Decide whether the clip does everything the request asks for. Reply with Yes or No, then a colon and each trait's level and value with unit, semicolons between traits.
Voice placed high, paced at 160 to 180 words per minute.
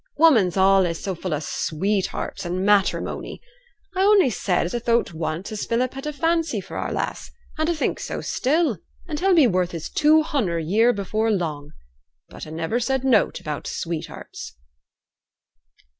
Yes: high, 210 Hz; average, 175 wpm